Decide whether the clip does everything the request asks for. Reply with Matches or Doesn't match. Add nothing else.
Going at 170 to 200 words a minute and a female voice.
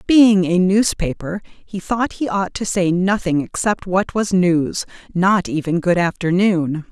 Doesn't match